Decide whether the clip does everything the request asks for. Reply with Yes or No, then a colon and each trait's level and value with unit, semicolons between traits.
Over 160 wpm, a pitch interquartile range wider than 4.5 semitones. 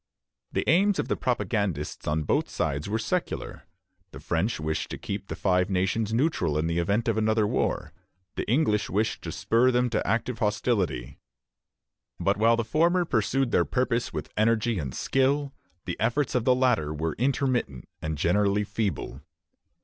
Yes: average, 170 wpm; average, 5.2 semitones